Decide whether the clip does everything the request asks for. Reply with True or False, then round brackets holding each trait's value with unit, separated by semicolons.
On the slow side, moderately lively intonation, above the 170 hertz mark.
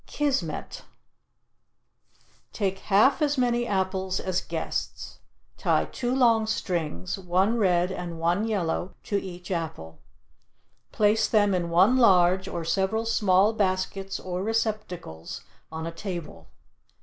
True (120 wpm; 3.7 semitones; 190 Hz)